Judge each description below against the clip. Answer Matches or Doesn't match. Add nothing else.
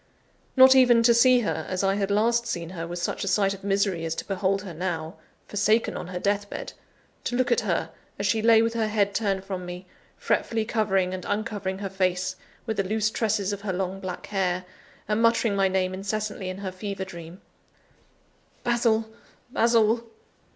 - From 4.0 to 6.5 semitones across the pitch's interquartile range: Doesn't match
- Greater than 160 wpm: Matches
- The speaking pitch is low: Doesn't match